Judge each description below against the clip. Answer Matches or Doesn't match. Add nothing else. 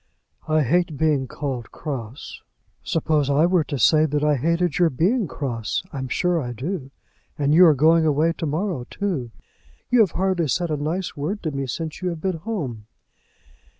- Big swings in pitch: Doesn't match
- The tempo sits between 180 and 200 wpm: Matches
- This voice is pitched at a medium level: Matches